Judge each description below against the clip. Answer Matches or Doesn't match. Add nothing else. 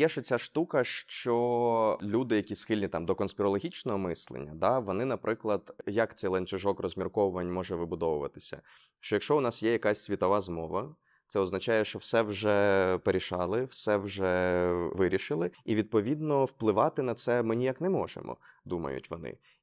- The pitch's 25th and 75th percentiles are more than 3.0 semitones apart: Matches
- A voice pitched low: Matches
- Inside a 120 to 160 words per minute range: Matches